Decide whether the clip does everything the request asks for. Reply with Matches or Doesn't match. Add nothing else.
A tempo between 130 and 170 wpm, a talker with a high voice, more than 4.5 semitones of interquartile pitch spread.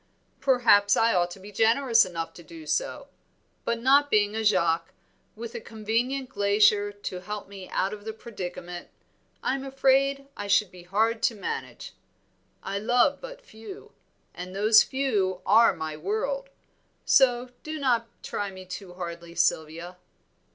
Matches